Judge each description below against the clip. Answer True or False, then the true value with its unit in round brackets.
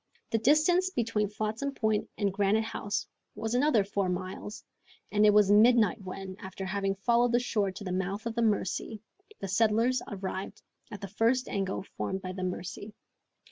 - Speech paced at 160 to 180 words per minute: True (175 wpm)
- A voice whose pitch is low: False (210 Hz)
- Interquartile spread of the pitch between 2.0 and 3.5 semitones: True (2.9 semitones)